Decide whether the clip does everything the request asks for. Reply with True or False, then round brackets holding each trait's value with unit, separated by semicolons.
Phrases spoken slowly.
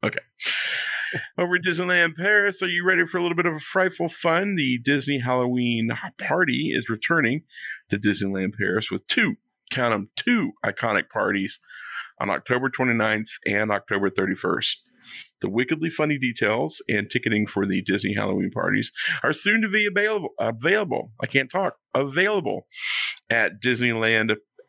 False (150 wpm)